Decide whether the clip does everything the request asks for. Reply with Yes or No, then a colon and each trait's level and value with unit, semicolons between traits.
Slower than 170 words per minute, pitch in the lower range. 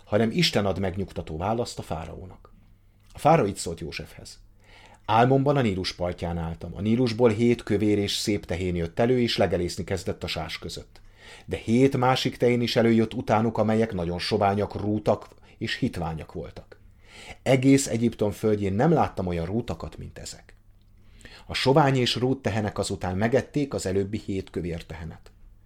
Yes: average, 155 wpm; low, 100 Hz